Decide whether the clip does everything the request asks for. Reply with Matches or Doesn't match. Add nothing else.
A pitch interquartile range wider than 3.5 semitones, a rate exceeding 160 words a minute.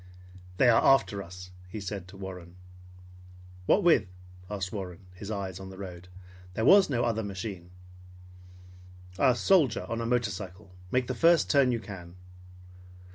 Doesn't match